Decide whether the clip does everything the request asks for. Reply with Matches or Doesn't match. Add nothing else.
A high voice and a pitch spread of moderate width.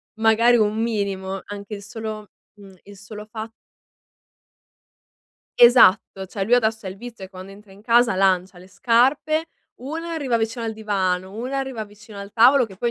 Matches